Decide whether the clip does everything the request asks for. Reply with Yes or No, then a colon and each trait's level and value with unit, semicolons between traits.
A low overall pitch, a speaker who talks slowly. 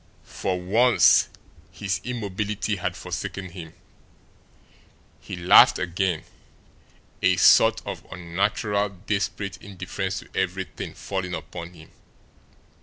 Yes: very low, 95 Hz; slow, 100 wpm